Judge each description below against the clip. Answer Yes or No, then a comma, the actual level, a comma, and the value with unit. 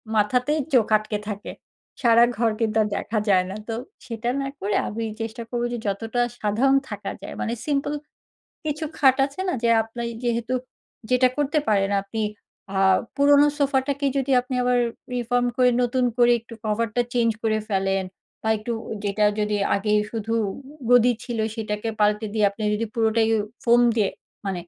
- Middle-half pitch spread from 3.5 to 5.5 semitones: No, average, 2.9 semitones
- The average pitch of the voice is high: Yes, high, 230 Hz